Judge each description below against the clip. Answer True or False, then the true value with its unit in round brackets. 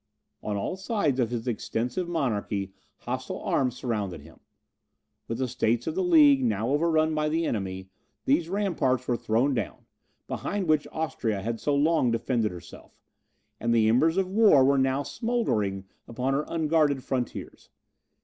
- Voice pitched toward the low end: True (130 Hz)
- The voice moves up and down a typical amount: False (6.0 semitones)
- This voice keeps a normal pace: True (155 wpm)